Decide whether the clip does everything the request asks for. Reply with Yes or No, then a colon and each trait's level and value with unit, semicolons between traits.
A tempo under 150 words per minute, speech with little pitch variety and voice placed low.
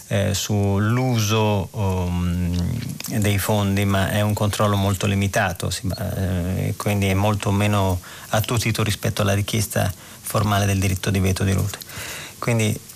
Yes: average, 140 wpm; narrow, 1.8 semitones; low, 105 Hz